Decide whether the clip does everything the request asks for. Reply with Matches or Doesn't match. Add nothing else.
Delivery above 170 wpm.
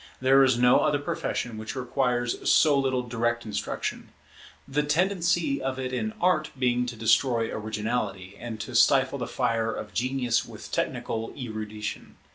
Doesn't match